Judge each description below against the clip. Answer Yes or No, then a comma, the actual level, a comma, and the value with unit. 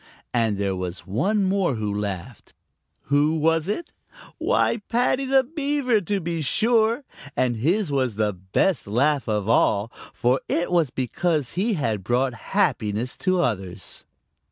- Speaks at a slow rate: No, average, 145 wpm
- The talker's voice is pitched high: No, medium, 140 Hz